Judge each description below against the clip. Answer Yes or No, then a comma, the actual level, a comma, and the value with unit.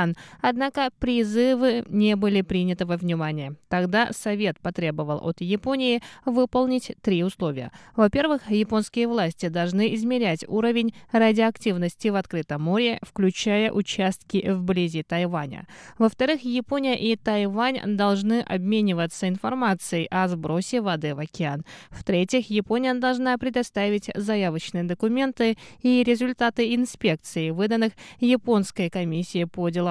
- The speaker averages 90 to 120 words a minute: Yes, slow, 110 wpm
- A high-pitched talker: Yes, high, 210 Hz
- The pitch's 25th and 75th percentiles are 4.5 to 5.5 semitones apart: Yes, average, 5.0 semitones